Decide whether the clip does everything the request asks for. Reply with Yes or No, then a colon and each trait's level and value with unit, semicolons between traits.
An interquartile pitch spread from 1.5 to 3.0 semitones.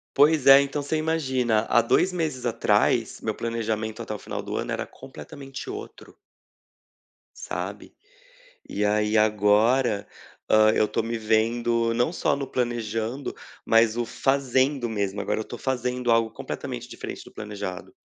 No: average, 3.5 semitones